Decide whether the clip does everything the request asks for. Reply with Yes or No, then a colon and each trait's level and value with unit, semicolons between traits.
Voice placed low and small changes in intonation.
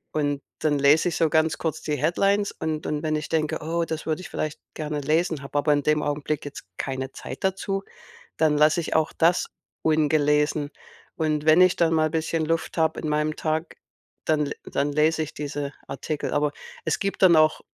No: medium, 155 Hz; narrow, 1.4 semitones